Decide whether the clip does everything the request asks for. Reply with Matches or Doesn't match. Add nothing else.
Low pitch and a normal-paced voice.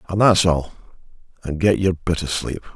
Matches